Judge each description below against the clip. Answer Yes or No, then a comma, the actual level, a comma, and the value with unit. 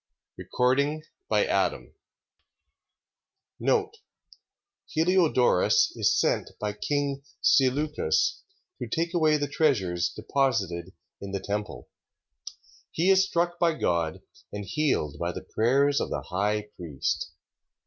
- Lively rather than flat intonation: Yes, wide, 7.8 semitones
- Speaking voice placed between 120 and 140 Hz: Yes, low, 135 Hz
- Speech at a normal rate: No, slow, 110 wpm